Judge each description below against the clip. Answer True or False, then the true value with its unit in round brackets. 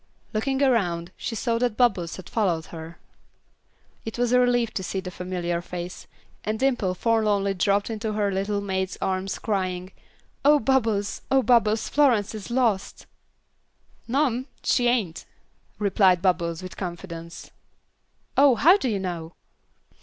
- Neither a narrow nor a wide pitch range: True (4.7 semitones)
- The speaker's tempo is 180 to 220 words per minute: False (145 wpm)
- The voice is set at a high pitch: True (205 Hz)